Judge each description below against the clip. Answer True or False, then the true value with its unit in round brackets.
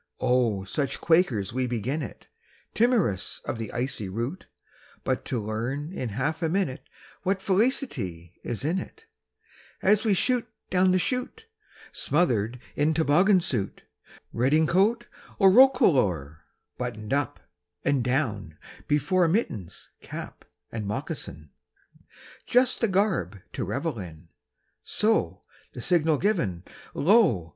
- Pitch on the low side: False (145 Hz)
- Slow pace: True (120 wpm)